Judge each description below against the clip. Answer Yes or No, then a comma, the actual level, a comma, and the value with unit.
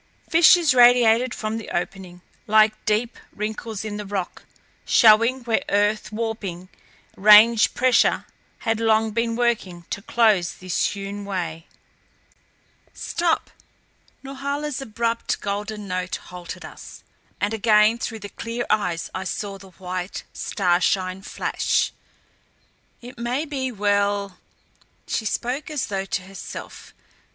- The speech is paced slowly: Yes, slow, 125 wpm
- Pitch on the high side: Yes, high, 215 Hz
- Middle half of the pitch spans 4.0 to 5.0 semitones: No, average, 3.2 semitones